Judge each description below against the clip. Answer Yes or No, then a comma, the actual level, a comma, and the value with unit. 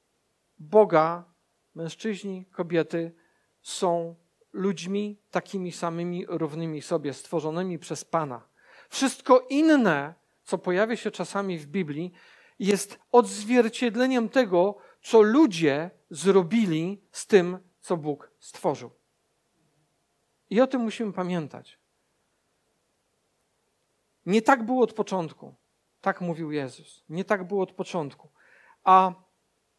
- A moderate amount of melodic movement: Yes, average, 4.3 semitones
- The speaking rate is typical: No, slow, 100 wpm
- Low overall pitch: No, medium, 185 Hz